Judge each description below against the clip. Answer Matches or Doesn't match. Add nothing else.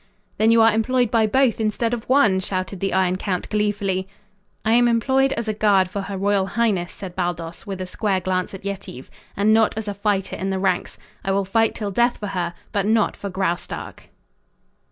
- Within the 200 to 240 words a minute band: Matches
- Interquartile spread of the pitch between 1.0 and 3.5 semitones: Matches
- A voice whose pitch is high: Matches